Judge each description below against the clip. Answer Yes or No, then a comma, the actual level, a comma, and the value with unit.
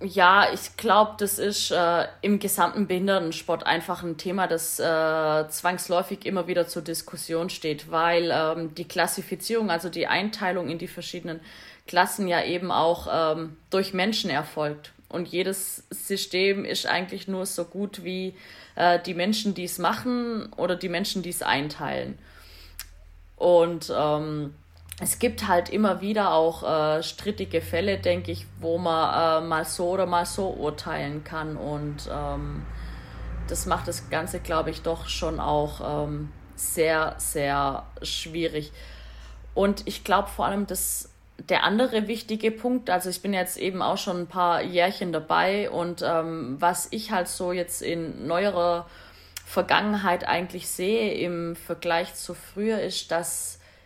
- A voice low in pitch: No, medium, 175 Hz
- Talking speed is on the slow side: No, average, 150 wpm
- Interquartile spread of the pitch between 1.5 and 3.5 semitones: Yes, average, 2.9 semitones